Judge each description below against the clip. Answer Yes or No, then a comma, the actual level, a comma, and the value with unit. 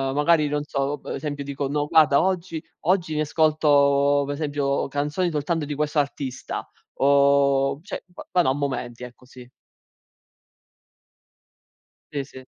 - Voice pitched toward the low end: No, medium, 145 Hz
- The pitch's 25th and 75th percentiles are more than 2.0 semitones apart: No, narrow, 1.7 semitones